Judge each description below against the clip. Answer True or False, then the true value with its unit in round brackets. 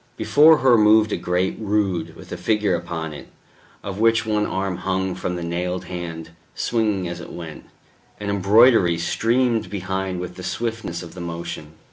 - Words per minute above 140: True (170 wpm)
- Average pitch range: True (3.7 semitones)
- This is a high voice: False (95 Hz)